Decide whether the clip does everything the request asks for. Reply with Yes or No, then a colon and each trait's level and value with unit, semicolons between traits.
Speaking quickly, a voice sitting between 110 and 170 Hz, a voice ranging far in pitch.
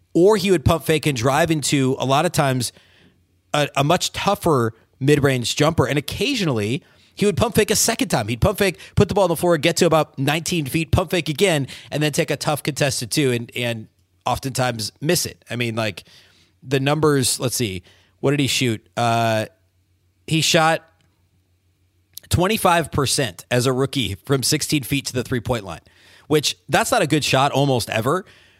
No: average, 190 wpm; low, 135 Hz; wide, 5.9 semitones